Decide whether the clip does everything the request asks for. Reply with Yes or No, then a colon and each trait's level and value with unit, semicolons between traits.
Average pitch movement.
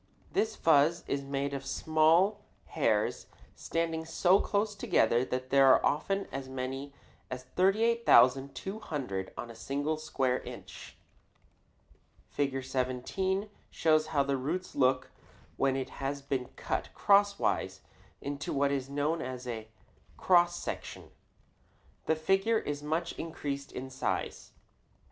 Yes: average, 4.3 semitones